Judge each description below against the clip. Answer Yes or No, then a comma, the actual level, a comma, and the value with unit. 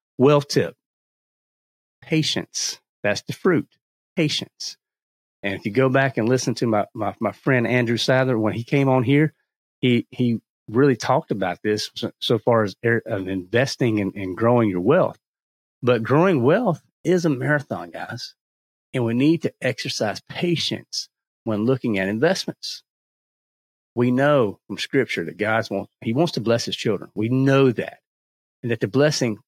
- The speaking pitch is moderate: No, low, 120 Hz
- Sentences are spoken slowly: No, average, 155 wpm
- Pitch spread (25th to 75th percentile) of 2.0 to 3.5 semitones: No, average, 4.3 semitones